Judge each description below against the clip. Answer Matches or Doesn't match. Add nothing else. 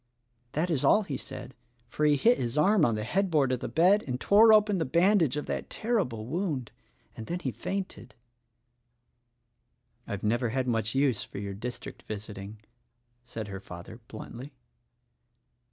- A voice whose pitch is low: Matches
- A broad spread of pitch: Matches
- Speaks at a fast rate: Doesn't match